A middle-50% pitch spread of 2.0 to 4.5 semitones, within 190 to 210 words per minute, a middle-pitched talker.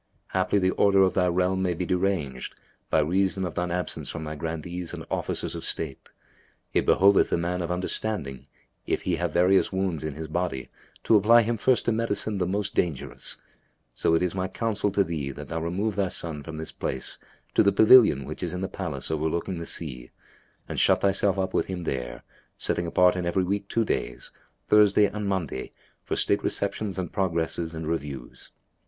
No: average, 3.4 semitones; average, 195 wpm; very low, 90 Hz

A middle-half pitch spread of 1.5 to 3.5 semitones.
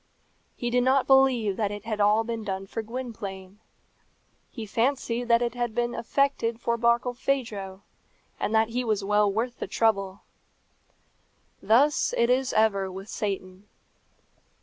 Yes: average, 3.0 semitones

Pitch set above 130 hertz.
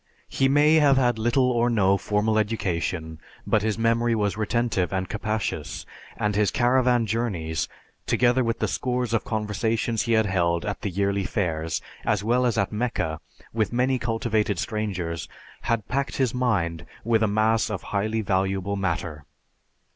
No: low, 110 Hz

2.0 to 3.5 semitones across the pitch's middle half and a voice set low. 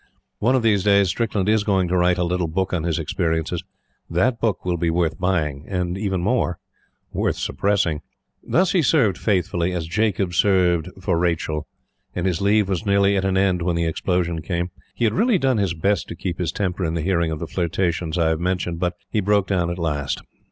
Yes: average, 2.9 semitones; very low, 90 Hz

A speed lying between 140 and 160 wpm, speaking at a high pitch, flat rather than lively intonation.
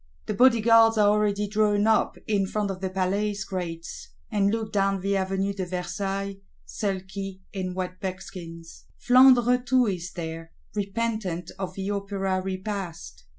Yes: average, 145 wpm; high, 195 Hz; narrow, 2.2 semitones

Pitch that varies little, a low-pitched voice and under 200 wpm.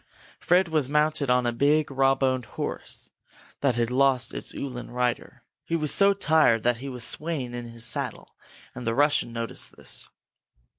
No: average, 3.7 semitones; low, 130 Hz; average, 170 wpm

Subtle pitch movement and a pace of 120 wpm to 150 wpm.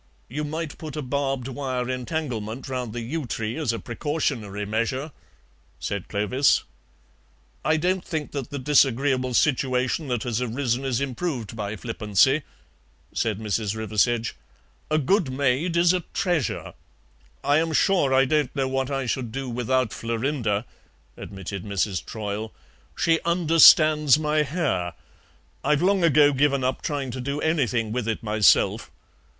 No: average, 4.7 semitones; average, 145 wpm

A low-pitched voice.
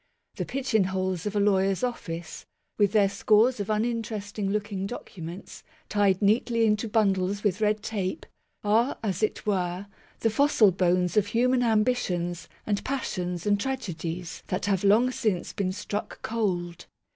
No: high, 205 Hz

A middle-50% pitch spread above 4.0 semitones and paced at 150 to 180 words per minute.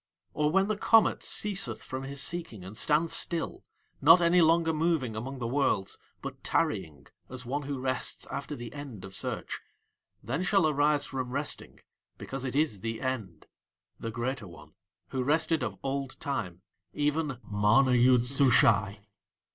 Yes: average, 4.7 semitones; average, 155 wpm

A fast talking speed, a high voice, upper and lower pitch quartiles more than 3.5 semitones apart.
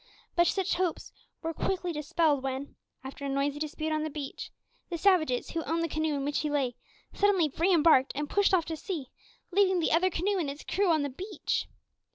Yes: fast, 210 wpm; very high, 315 Hz; average, 3.9 semitones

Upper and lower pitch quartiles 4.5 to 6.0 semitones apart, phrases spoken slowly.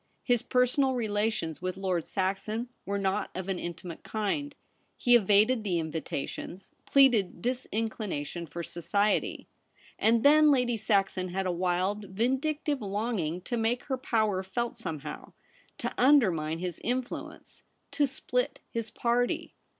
Yes: average, 5.0 semitones; slow, 130 wpm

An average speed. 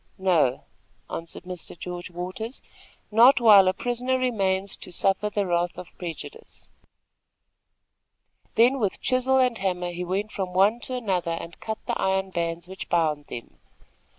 Yes: average, 150 wpm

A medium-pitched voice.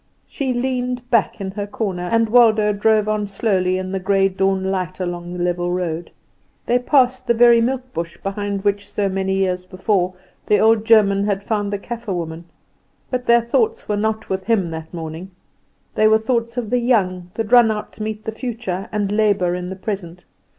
No: high, 205 Hz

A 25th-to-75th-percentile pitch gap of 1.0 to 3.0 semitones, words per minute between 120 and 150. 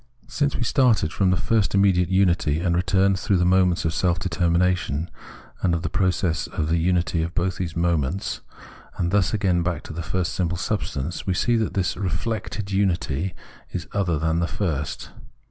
No: narrow, 2.4 semitones; average, 180 wpm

